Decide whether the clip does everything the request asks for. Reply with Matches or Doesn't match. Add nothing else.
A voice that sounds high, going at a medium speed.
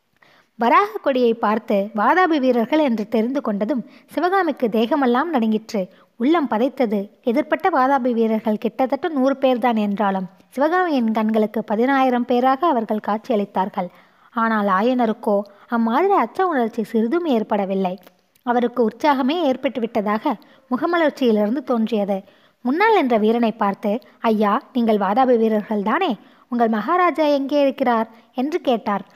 Matches